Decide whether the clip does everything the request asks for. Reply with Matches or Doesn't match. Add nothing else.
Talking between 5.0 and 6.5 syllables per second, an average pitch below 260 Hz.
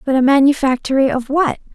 Doesn't match